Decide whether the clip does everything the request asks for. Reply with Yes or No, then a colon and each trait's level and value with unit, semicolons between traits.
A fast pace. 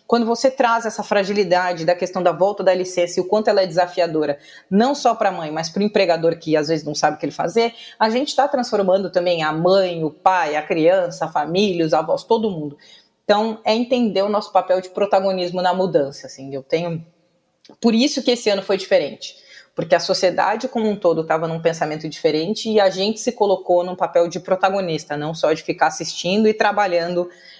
Yes: fast, 215 wpm